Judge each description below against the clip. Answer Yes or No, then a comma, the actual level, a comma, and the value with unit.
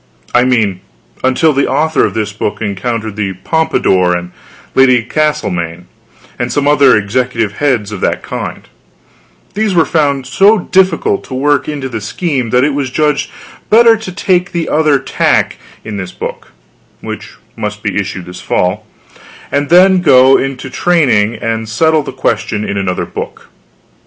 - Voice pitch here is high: No, low, 130 Hz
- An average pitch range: No, wide, 6.7 semitones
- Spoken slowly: No, average, 155 wpm